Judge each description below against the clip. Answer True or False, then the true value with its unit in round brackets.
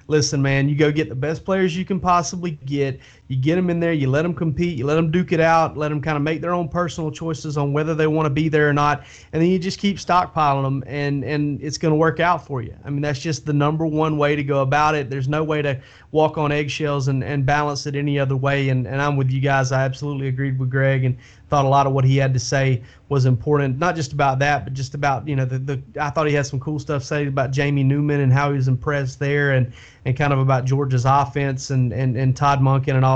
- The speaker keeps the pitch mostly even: True (2.3 semitones)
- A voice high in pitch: False (145 Hz)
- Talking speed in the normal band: False (275 wpm)